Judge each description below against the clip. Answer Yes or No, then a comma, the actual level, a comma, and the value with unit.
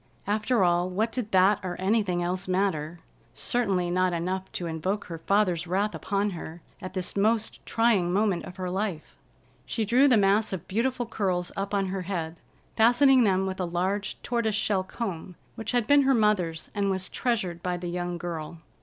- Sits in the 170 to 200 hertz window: Yes, high, 190 Hz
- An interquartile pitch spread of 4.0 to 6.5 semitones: No, average, 3.3 semitones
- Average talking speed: Yes, average, 185 wpm